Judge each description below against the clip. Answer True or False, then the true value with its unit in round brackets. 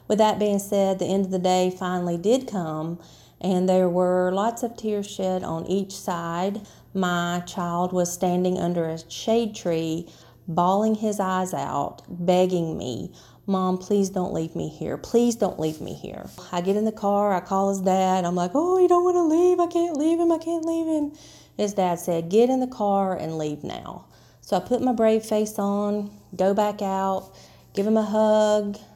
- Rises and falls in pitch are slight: False (3.1 semitones)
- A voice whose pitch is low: False (195 Hz)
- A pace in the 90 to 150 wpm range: False (200 wpm)